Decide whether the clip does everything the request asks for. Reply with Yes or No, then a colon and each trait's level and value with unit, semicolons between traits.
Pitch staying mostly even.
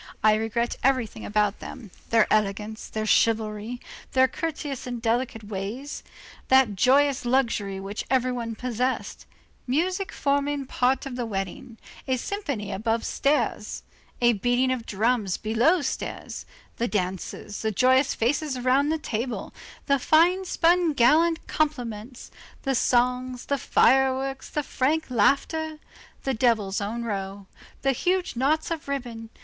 No: average, 4.1 semitones